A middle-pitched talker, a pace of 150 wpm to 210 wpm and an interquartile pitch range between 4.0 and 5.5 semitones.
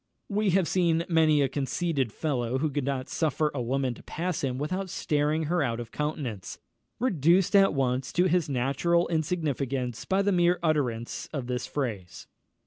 Yes: medium, 150 Hz; average, 170 wpm; average, 4.9 semitones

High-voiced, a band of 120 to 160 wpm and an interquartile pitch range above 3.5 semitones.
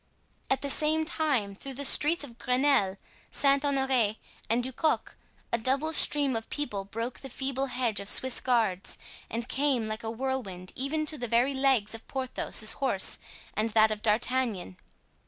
No: very high, 255 Hz; average, 170 wpm; average, 3.9 semitones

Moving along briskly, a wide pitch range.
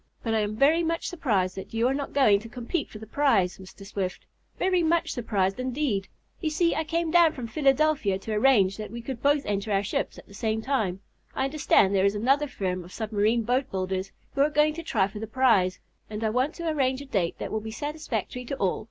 Yes: fast, 235 wpm; wide, 6.1 semitones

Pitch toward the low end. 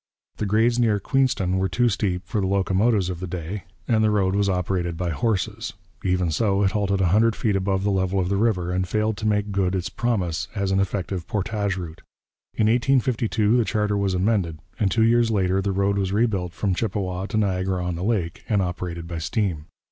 Yes: low, 100 Hz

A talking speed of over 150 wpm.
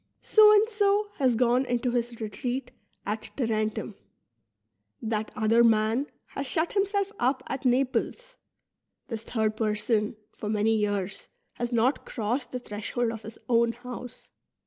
No: average, 145 wpm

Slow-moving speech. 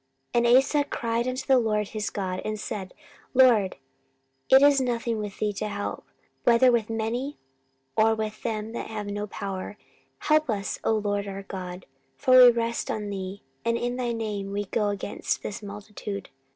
No: average, 180 wpm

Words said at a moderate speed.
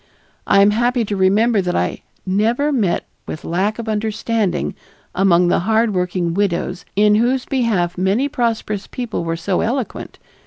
Yes: average, 155 wpm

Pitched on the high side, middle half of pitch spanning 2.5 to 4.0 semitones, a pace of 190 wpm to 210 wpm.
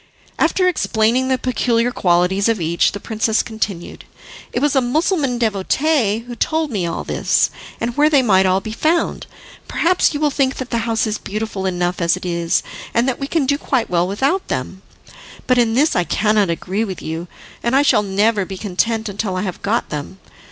No: high, 220 Hz; wide, 5.5 semitones; average, 200 wpm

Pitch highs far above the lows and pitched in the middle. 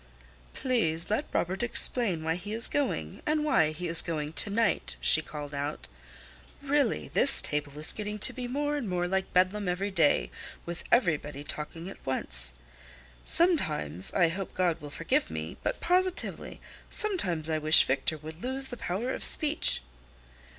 Yes: wide, 7.9 semitones; medium, 180 Hz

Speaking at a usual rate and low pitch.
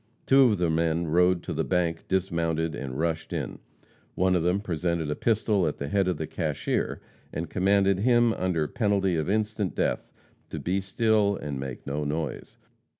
Yes: average, 180 wpm; very low, 90 Hz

